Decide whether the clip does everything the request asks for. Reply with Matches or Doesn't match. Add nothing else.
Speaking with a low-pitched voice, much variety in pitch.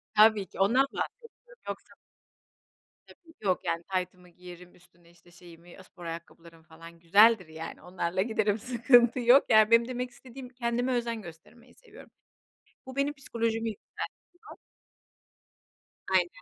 Doesn't match